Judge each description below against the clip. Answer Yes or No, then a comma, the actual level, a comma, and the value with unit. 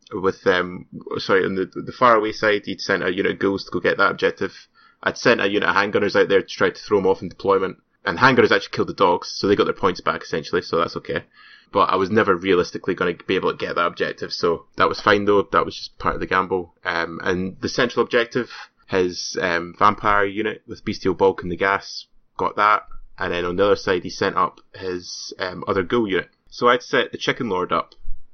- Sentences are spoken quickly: Yes, fast, 245 wpm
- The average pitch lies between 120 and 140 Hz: No, low, 100 Hz